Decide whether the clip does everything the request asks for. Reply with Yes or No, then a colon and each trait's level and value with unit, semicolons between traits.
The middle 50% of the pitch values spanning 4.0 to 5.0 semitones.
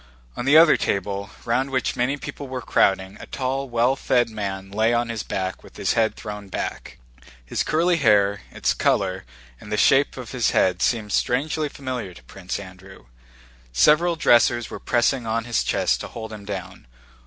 Yes: average, 4.7 semitones